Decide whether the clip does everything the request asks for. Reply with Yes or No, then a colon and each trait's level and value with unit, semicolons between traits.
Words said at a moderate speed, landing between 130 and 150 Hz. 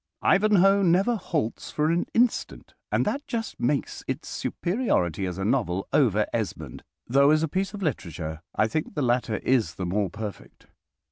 Yes: average, 165 wpm; medium, 140 Hz